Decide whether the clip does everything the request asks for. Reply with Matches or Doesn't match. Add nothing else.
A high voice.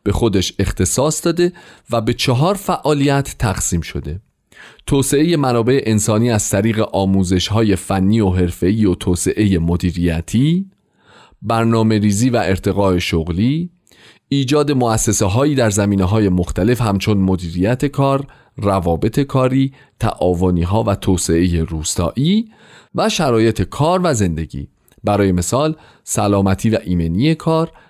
Doesn't match